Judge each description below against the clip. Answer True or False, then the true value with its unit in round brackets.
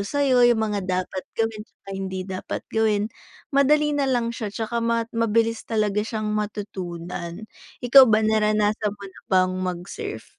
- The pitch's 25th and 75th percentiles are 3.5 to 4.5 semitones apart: False (2.8 semitones)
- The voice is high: True (215 Hz)